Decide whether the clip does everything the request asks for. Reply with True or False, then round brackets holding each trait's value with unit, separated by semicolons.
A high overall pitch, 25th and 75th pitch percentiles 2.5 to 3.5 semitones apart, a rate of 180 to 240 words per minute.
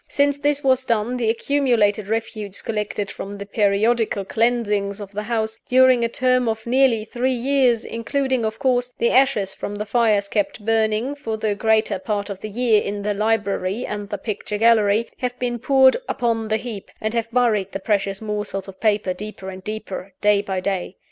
True (220 Hz; 2.9 semitones; 190 wpm)